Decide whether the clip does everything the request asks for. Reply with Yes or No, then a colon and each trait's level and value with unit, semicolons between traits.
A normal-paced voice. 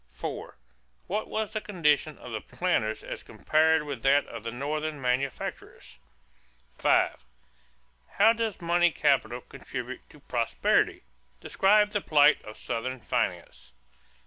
No: slow, 125 wpm